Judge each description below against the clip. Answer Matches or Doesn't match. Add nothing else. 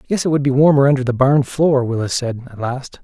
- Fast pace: Matches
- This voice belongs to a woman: Doesn't match